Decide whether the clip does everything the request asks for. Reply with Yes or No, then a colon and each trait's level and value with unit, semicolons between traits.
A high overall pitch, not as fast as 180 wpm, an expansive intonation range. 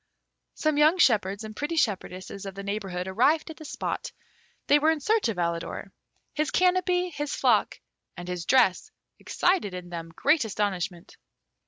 Yes: high, 220 Hz; average, 160 wpm; wide, 8.7 semitones